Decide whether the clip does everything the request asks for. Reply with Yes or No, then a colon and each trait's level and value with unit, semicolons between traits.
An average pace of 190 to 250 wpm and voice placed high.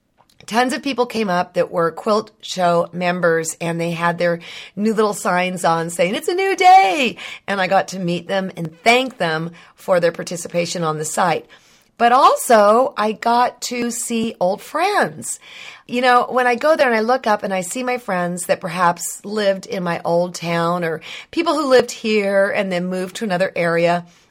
Yes: average, 195 wpm; high, 195 Hz